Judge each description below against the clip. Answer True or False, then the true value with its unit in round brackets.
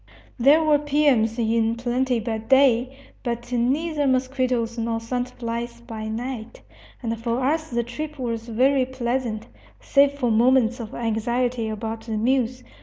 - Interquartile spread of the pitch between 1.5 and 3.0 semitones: True (2.4 semitones)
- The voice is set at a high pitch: True (240 Hz)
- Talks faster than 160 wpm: False (145 wpm)